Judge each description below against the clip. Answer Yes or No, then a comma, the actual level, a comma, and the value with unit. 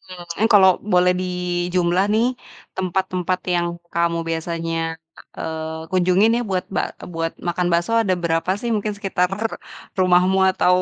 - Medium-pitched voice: Yes, medium, 180 Hz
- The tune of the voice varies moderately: No, narrow, 1.7 semitones